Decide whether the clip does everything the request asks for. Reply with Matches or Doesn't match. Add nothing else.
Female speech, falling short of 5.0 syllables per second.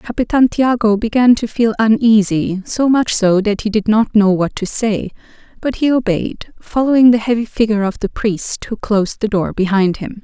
Matches